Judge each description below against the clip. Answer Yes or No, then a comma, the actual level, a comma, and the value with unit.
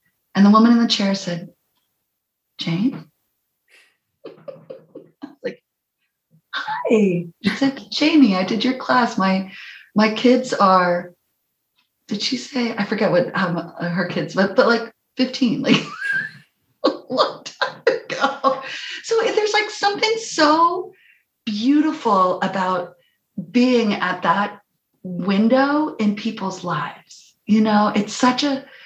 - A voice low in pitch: No, high, 225 Hz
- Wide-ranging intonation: Yes, wide, 6.2 semitones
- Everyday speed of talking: No, slow, 125 wpm